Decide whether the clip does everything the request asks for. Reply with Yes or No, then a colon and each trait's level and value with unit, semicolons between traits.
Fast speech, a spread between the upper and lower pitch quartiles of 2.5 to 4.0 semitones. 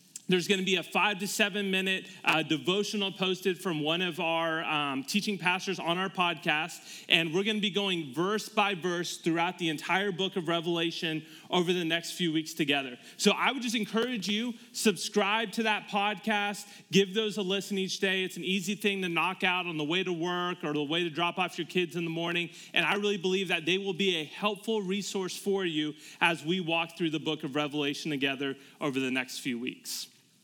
Yes: fast, 215 wpm; average, 3.4 semitones